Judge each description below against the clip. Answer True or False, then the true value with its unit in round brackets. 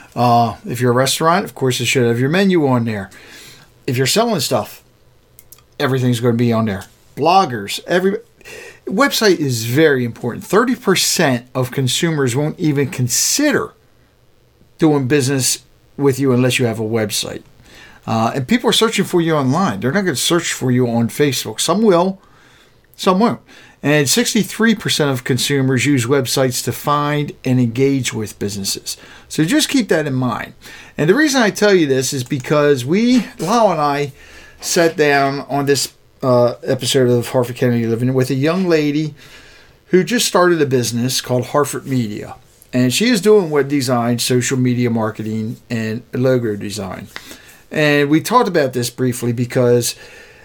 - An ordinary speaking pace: True (165 wpm)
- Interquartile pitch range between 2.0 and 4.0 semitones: False (4.8 semitones)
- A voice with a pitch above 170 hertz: False (135 Hz)